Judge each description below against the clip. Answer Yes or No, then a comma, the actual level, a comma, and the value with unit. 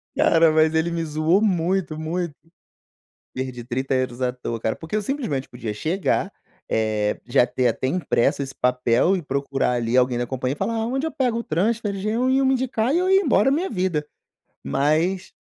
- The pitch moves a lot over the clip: Yes, wide, 8.3 semitones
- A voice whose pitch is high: No, medium, 160 Hz